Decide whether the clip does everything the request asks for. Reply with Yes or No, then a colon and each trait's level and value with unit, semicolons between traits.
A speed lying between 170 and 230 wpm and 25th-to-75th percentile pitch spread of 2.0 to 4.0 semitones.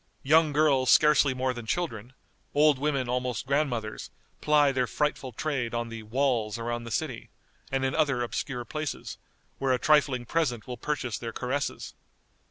No: average, 160 wpm; average, 3.7 semitones